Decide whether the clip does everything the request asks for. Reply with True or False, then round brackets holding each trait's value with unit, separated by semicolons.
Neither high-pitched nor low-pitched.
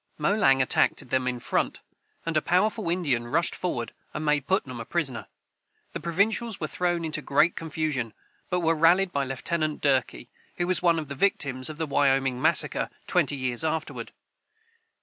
True (155 Hz)